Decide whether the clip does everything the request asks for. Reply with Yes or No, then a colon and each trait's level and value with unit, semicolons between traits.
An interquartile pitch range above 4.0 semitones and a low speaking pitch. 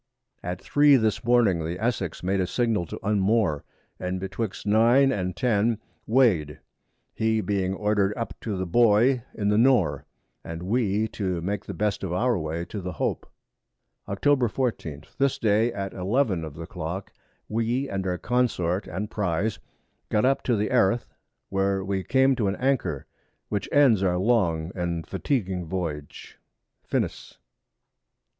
Yes: average, 4.4 semitones; low, 100 Hz